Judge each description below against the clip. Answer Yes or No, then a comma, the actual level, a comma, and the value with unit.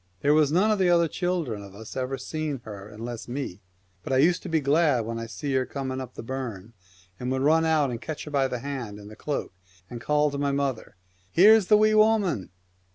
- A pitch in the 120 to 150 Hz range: Yes, low, 135 Hz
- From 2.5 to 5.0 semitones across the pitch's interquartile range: No, wide, 5.5 semitones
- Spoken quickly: Yes, fast, 235 wpm